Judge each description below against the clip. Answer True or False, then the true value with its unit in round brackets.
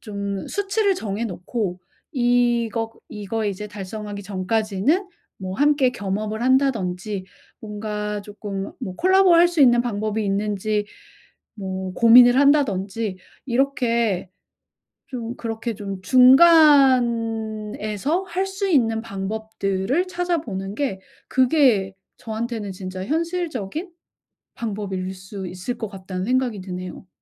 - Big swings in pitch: False (4.6 semitones)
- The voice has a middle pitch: False (220 Hz)